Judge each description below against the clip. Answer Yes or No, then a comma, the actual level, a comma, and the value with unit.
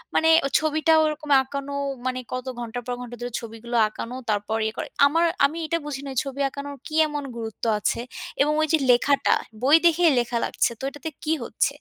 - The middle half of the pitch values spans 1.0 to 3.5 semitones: No, average, 4.1 semitones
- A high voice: Yes, very high, 280 Hz